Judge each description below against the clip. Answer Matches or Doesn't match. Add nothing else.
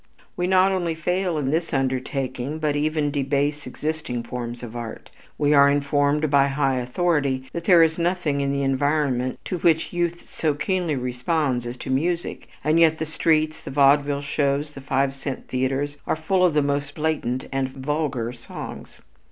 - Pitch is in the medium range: Matches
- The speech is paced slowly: Doesn't match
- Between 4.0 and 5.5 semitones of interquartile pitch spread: Doesn't match